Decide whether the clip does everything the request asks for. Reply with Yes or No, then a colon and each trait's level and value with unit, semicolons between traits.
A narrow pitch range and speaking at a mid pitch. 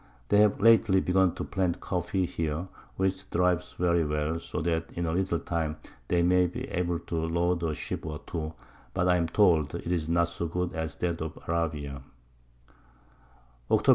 No: narrow, 1.8 semitones; very low, 85 Hz